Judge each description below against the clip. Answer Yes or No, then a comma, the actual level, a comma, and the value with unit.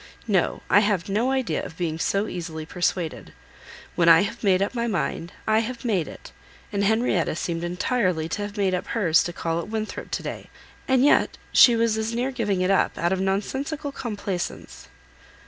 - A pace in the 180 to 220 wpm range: Yes, average, 190 wpm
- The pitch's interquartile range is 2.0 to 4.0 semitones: No, average, 4.7 semitones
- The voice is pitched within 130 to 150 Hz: No, high, 200 Hz